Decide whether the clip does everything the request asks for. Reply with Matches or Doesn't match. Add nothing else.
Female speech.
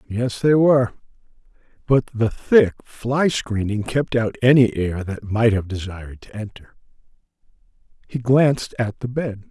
Doesn't match